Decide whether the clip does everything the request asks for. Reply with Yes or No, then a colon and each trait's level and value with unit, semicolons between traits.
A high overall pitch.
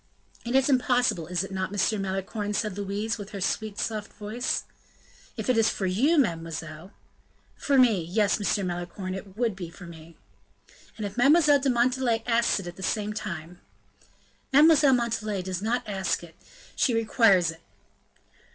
Yes: high, 210 Hz